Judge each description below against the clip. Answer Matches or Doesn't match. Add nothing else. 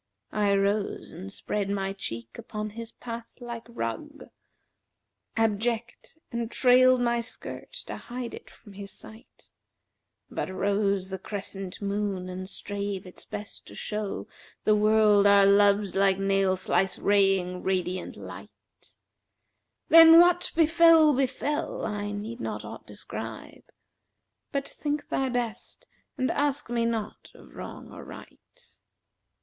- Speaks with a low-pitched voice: Doesn't match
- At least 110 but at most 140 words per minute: Matches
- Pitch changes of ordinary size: Matches